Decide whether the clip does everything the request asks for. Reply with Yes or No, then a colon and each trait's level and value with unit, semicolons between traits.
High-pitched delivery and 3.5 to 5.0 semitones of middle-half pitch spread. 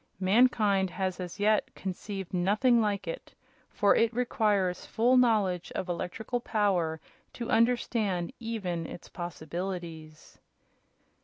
Yes: high, 200 Hz; average, 4.2 semitones